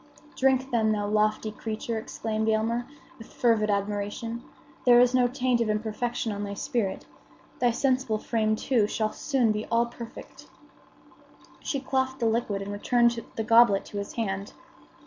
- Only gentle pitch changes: Yes, narrow, 2.2 semitones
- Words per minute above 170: No, average, 155 wpm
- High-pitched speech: Yes, high, 225 Hz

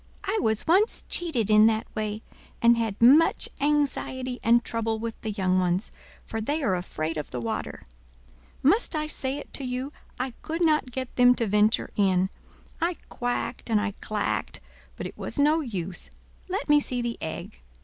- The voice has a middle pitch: No, high, 235 Hz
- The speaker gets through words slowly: No, average, 180 wpm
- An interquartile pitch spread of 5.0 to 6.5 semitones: Yes, wide, 5.5 semitones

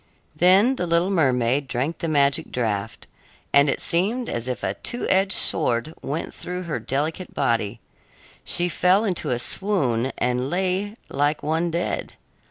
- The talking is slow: No, average, 155 wpm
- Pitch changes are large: Yes, wide, 6.3 semitones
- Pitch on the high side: No, medium, 155 Hz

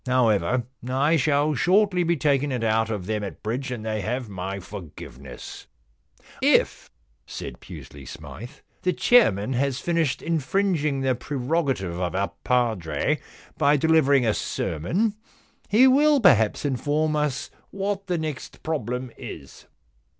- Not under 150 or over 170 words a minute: No, average, 140 wpm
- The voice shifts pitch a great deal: Yes, wide, 6.7 semitones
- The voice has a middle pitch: No, low, 130 Hz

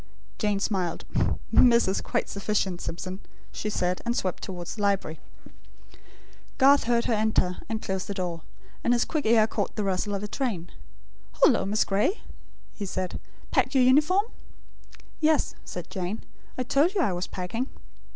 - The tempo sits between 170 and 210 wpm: No, average, 160 wpm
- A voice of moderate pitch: No, high, 210 Hz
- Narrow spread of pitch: No, average, 4.6 semitones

